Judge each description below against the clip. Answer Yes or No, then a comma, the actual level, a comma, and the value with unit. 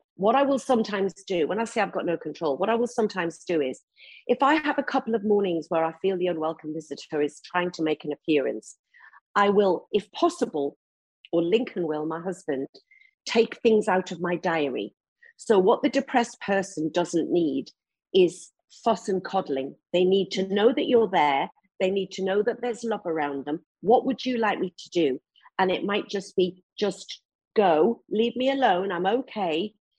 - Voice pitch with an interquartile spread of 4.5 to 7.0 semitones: Yes, wide, 5.6 semitones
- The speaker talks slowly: No, average, 195 wpm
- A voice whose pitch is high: Yes, high, 195 Hz